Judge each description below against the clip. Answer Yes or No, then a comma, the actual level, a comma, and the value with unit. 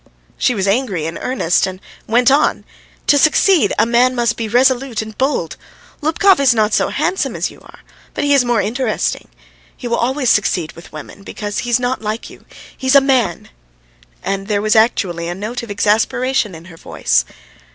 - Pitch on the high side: Yes, high, 230 Hz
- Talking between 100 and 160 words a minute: No, average, 190 wpm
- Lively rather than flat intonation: No, average, 4.6 semitones